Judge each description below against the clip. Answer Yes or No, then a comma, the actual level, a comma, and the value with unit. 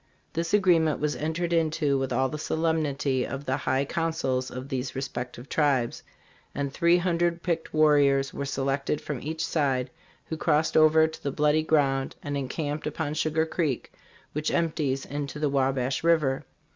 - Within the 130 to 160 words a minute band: No, average, 170 wpm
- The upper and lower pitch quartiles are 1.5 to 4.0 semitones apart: Yes, average, 2.8 semitones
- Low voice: No, medium, 150 Hz